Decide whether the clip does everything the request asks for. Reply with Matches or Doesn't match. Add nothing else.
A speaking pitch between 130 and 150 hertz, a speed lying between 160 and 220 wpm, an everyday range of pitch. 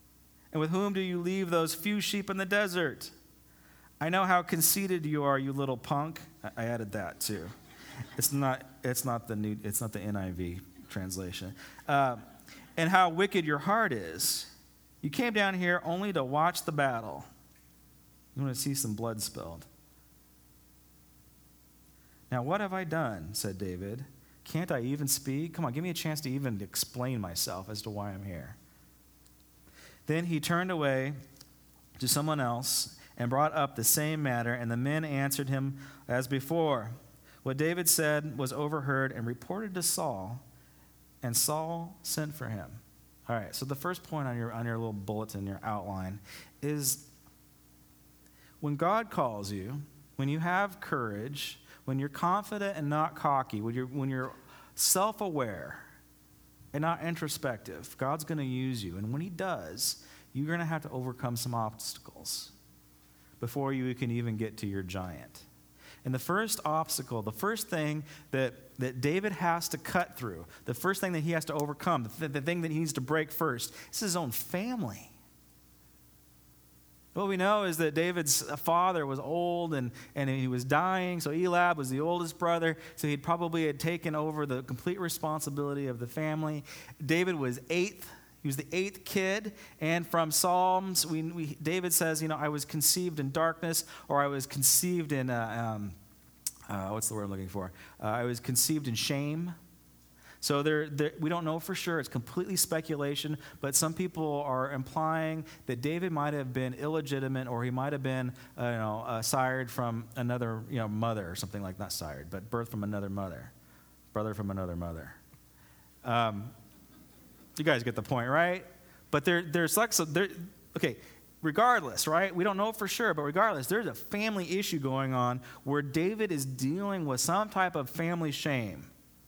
Doesn't match